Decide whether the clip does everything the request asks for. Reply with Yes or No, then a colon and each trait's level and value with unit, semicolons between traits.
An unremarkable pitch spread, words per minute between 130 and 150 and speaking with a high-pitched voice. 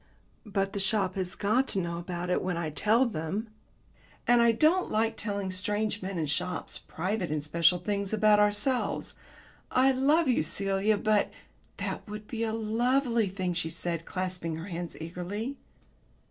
No: average, 3.8 semitones; average, 170 wpm; high, 200 Hz